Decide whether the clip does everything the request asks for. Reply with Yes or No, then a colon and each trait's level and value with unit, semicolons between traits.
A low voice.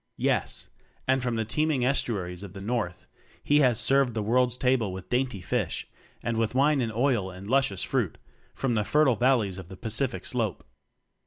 Yes: low, 120 Hz